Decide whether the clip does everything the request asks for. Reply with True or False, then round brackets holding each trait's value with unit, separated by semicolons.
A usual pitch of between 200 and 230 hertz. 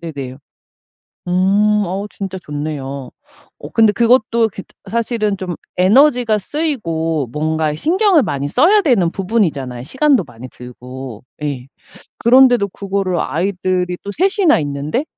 False (185 Hz)